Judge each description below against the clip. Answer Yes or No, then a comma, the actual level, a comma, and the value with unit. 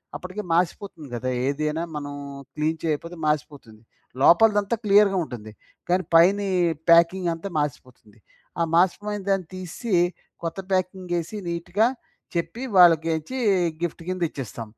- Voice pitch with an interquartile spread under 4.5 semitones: Yes, average, 4.0 semitones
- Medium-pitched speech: Yes, medium, 170 Hz